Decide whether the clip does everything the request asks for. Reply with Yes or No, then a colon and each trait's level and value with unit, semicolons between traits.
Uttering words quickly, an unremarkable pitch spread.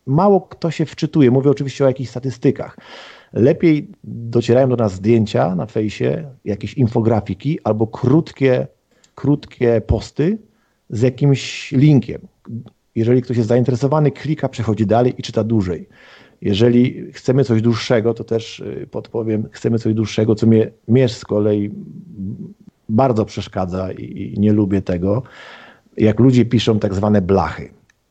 No: average, 130 wpm; average, 3.8 semitones